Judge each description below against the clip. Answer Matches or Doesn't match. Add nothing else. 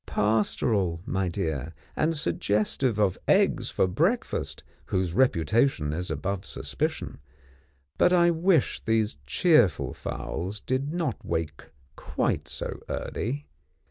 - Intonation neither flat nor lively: Doesn't match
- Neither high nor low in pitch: Doesn't match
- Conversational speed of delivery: Doesn't match